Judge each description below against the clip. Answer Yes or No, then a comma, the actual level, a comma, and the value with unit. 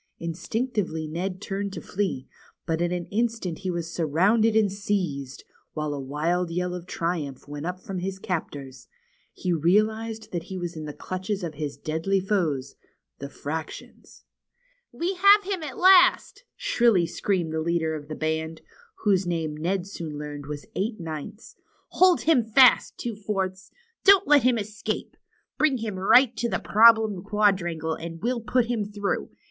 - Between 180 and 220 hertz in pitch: Yes, medium, 185 Hz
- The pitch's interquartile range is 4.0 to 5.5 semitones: Yes, average, 5.2 semitones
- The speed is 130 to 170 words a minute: Yes, average, 165 wpm